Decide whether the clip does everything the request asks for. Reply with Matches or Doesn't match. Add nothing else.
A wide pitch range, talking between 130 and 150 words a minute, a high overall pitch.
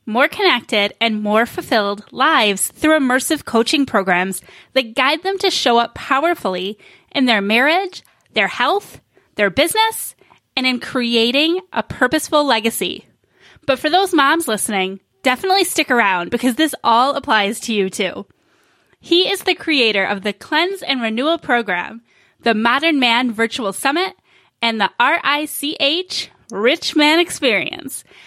Matches